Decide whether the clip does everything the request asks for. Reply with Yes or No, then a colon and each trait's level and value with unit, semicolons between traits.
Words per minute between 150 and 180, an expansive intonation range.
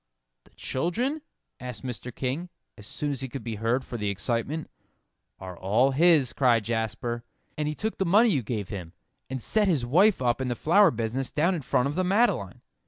No: average, 200 wpm; wide, 6.5 semitones